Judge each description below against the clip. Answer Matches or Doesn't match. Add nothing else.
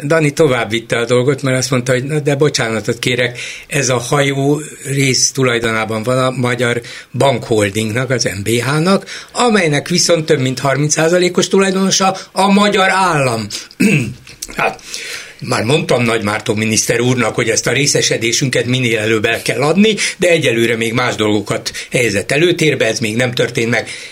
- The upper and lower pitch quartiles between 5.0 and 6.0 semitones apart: Matches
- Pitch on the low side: Matches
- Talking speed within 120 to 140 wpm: Doesn't match